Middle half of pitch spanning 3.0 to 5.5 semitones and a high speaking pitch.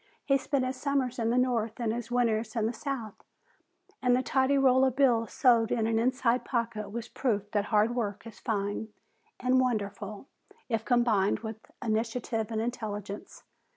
No: narrow, 2.6 semitones; high, 230 Hz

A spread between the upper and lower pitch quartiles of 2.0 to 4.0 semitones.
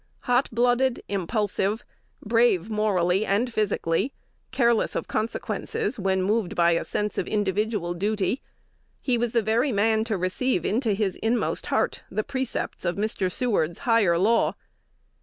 Yes: average, 3.5 semitones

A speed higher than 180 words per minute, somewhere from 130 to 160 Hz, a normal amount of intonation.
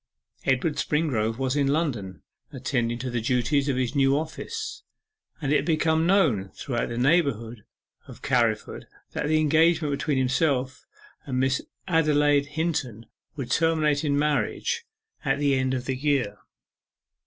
No: average, 145 wpm; medium, 140 Hz; average, 3.6 semitones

